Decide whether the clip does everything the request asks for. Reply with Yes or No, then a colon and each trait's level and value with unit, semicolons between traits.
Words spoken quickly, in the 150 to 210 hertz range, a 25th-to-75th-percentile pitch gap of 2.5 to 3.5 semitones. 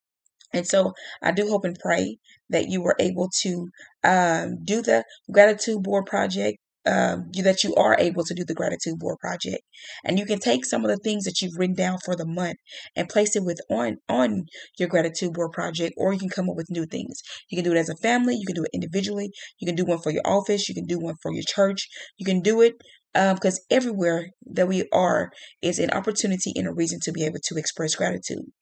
Yes: fast, 235 wpm; medium, 185 Hz; average, 2.9 semitones